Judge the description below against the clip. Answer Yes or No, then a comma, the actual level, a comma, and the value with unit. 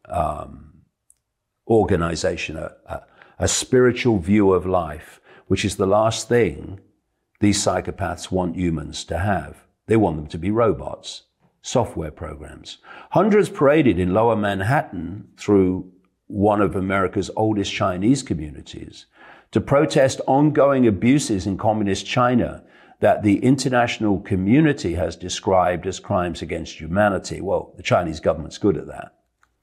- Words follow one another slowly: Yes, slow, 130 wpm